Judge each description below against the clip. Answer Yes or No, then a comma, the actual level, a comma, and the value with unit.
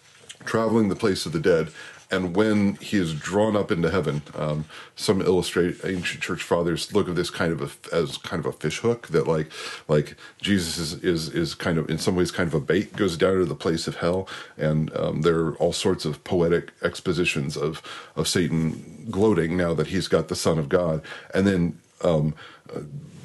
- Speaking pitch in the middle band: No, very low, 90 Hz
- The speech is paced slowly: No, fast, 205 wpm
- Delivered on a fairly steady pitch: No, average, 3.9 semitones